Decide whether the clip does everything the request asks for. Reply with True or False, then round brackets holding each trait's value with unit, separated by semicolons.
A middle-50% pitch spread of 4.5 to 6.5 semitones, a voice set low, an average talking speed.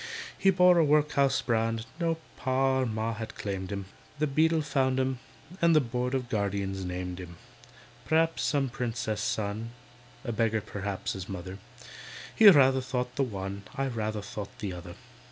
True (5.1 semitones; 115 Hz; 165 wpm)